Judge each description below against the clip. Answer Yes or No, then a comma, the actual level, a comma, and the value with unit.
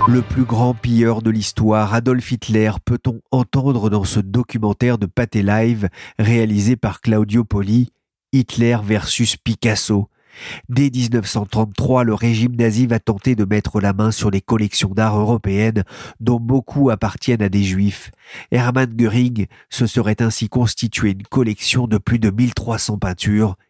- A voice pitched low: Yes, low, 115 Hz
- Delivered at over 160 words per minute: No, slow, 145 wpm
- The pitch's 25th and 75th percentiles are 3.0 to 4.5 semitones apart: No, narrow, 2.6 semitones